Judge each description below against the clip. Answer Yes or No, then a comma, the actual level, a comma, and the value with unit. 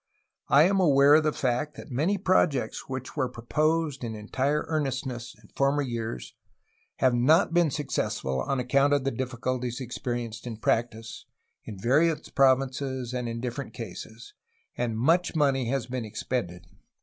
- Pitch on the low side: Yes, low, 130 Hz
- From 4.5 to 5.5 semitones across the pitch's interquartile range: No, average, 3.4 semitones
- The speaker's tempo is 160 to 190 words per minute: No, average, 150 wpm